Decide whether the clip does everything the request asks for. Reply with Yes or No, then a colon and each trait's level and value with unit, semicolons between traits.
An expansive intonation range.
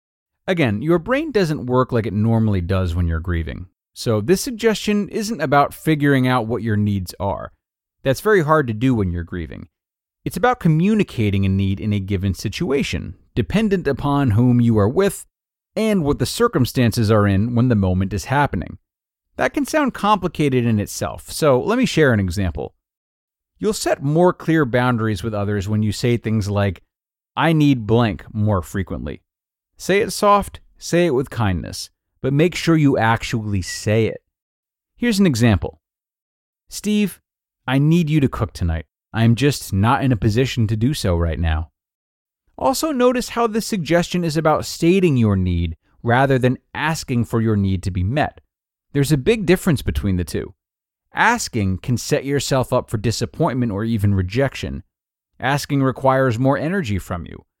Yes: wide, 7.9 semitones